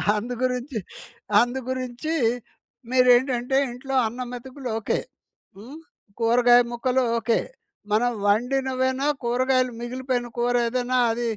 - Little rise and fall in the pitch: Yes, narrow, 1.3 semitones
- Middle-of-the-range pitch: No, very high, 250 Hz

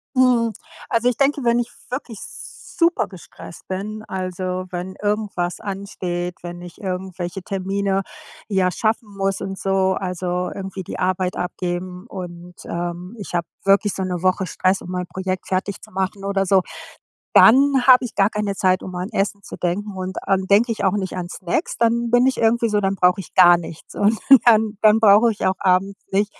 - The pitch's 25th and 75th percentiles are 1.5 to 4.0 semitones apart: Yes, average, 2.7 semitones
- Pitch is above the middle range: Yes, high, 195 Hz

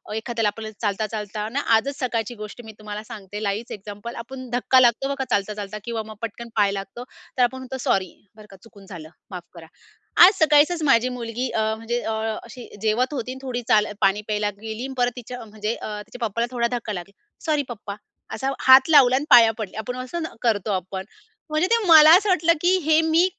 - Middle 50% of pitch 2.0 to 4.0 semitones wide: Yes, average, 3.6 semitones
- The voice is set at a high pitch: Yes, high, 230 Hz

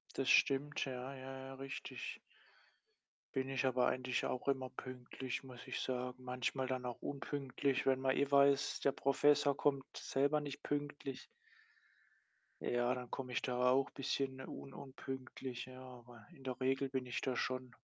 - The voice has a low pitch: Yes, low, 130 Hz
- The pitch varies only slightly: Yes, narrow, 1.4 semitones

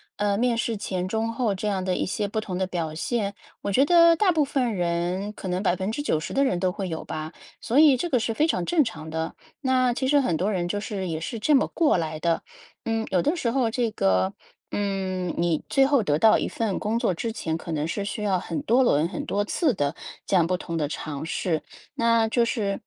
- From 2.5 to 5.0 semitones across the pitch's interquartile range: No, wide, 5.4 semitones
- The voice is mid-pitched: No, high, 200 Hz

